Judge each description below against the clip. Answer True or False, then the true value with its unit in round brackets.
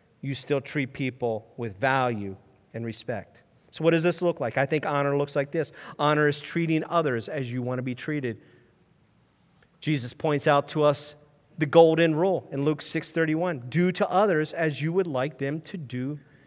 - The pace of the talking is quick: False (185 wpm)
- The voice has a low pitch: False (145 Hz)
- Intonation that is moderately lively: True (3.4 semitones)